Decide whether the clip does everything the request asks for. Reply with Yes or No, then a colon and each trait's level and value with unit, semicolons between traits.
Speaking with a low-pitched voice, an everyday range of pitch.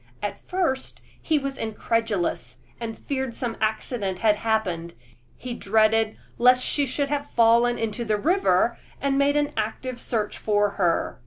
No: high, 230 Hz; average, 3.8 semitones